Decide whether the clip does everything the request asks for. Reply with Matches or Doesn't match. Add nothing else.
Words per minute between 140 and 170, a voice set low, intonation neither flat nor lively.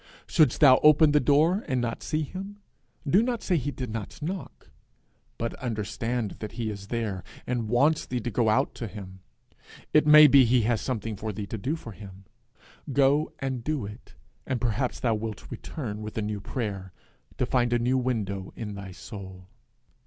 Doesn't match